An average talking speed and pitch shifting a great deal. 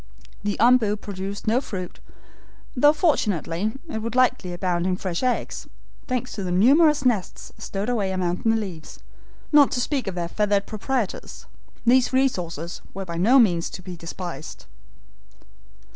Yes: average, 150 wpm; wide, 5.7 semitones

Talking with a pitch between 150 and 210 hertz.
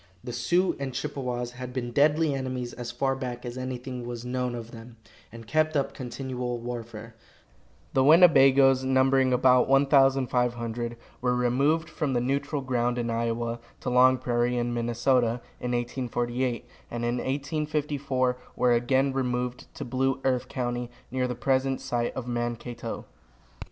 No: low, 125 Hz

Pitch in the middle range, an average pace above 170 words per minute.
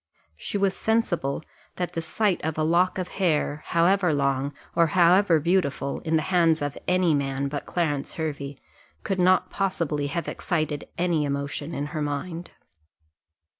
No: medium, 165 Hz; average, 155 wpm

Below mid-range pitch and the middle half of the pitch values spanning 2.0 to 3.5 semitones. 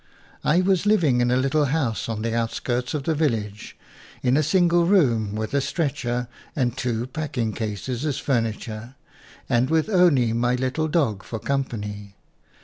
No: low, 125 Hz; average, 5.1 semitones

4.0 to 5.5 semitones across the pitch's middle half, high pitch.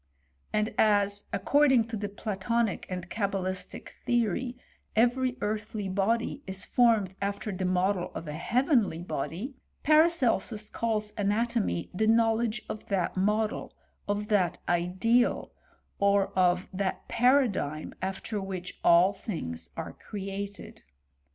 No: average, 3.5 semitones; high, 205 Hz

